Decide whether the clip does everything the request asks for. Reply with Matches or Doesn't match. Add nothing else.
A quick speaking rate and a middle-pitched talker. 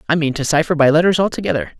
Matches